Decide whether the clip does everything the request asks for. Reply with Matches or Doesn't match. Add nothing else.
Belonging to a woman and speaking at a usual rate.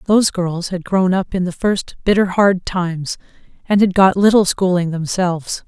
Matches